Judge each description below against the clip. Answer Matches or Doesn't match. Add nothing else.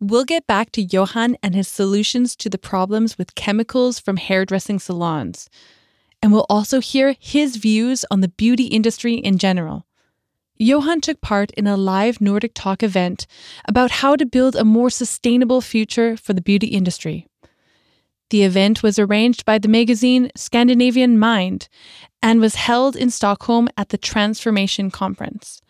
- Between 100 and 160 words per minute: Matches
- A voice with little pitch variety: Doesn't match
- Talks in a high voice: Matches